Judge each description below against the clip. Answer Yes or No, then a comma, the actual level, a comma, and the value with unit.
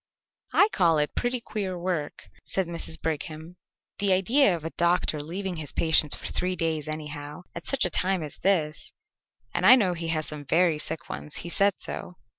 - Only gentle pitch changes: No, average, 3.4 semitones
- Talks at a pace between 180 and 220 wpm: Yes, average, 190 wpm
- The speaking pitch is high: No, medium, 170 Hz